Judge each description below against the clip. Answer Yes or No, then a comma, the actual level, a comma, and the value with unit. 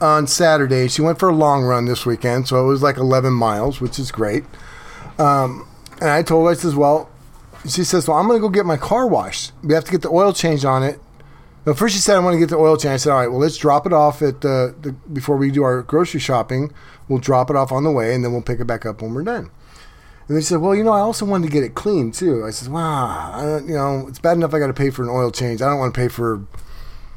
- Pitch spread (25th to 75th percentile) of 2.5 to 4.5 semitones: Yes, average, 3.9 semitones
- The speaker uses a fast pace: Yes, fast, 285 wpm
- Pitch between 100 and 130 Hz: No, medium, 140 Hz